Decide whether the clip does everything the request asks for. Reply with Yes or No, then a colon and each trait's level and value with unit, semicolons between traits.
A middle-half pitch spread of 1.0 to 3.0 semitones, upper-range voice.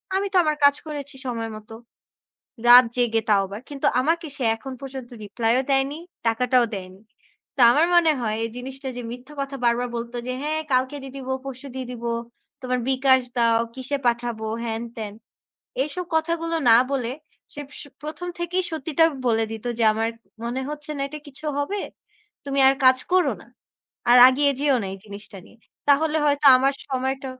No: average, 3.6 semitones; very high, 260 Hz